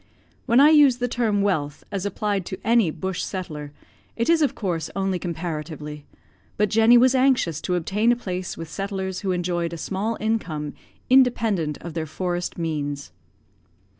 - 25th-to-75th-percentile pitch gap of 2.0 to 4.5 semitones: No, wide, 5.4 semitones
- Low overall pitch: No, high, 190 Hz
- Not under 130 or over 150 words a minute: No, average, 165 wpm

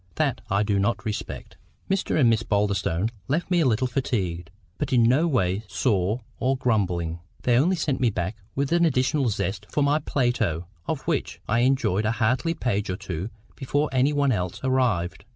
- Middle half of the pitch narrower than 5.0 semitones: No, wide, 5.4 semitones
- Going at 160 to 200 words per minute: Yes, average, 180 wpm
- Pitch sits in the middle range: No, low, 120 Hz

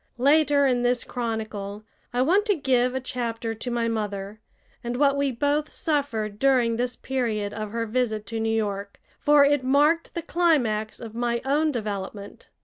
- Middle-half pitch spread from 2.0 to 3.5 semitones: No, average, 4.4 semitones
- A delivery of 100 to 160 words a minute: No, average, 170 wpm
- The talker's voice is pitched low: No, high, 240 Hz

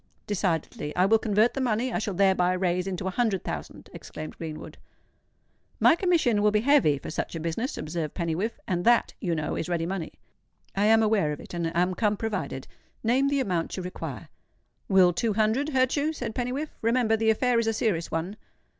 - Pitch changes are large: No, average, 4.9 semitones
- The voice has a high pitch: Yes, high, 205 Hz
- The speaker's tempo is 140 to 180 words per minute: No, average, 195 wpm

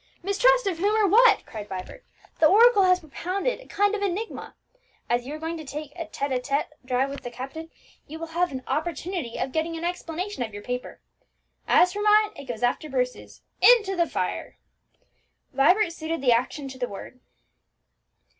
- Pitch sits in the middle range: No, very high, 325 Hz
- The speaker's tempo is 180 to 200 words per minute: Yes, average, 195 wpm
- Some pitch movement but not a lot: No, wide, 6.8 semitones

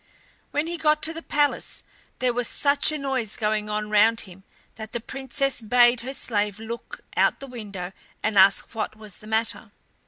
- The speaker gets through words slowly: No, average, 185 wpm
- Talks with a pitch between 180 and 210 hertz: No, high, 230 Hz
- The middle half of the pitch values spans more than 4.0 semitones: Yes, average, 4.4 semitones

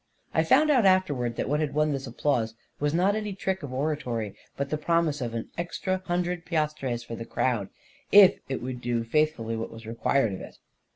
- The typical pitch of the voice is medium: Yes, medium, 145 Hz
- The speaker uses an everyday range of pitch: No, wide, 6.5 semitones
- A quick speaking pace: Yes, fast, 210 wpm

